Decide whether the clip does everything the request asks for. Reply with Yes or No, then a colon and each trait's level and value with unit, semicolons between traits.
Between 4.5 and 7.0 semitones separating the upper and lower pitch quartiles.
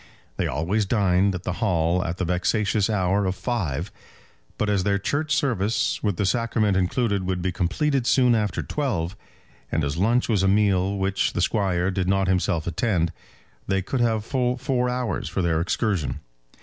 No: average, 3.8 semitones